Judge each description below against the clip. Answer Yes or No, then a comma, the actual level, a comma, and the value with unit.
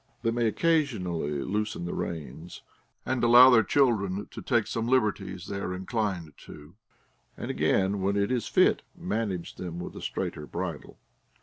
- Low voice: Yes, low, 100 Hz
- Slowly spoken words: No, average, 160 wpm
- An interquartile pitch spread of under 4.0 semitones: No, average, 4.8 semitones